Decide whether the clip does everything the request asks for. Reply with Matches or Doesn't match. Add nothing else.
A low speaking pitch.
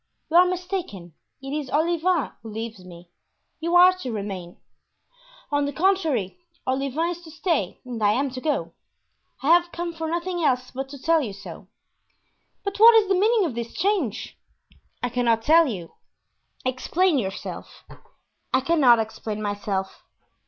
Doesn't match